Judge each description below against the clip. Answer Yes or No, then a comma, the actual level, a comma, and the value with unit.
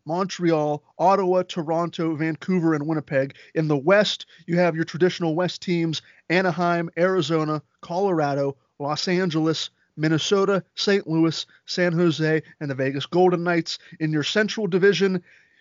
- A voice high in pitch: No, medium, 170 Hz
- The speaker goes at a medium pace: No, slow, 130 wpm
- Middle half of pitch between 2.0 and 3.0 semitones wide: Yes, narrow, 2.6 semitones